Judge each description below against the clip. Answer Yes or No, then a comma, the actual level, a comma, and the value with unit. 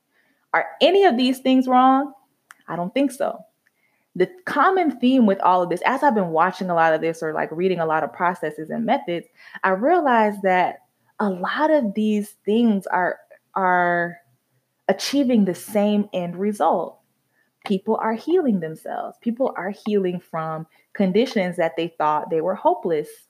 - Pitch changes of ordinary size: No, wide, 6.8 semitones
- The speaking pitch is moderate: No, high, 200 Hz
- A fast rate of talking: No, average, 165 wpm